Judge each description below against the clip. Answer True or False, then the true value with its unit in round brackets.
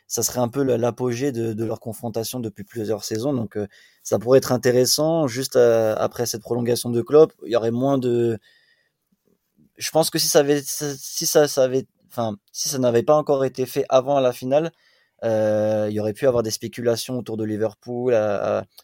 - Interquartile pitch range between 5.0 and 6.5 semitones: False (3.3 semitones)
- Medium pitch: False (120 Hz)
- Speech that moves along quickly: False (205 wpm)